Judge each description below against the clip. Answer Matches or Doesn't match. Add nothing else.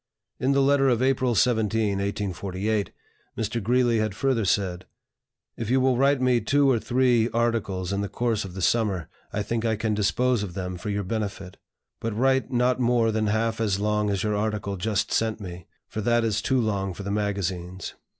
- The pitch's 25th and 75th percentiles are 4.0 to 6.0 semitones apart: Doesn't match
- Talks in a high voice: Doesn't match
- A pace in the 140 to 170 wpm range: Doesn't match